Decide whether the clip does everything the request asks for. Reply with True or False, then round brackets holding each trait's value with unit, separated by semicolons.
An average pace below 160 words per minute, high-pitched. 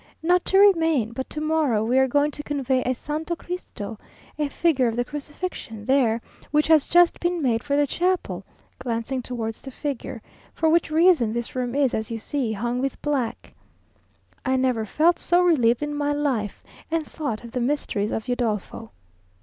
False (180 wpm; 270 Hz)